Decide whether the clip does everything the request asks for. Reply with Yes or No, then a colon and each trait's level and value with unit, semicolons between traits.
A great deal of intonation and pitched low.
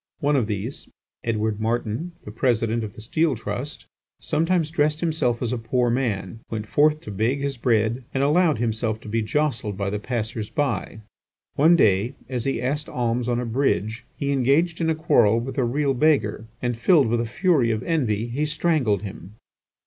No: average, 4.9 semitones; low, 120 Hz